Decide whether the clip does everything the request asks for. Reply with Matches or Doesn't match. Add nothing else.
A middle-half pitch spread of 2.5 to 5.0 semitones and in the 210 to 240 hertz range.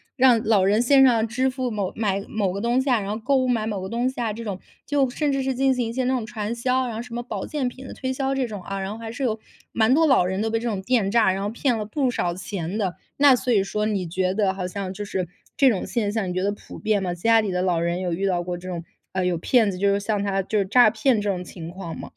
Matches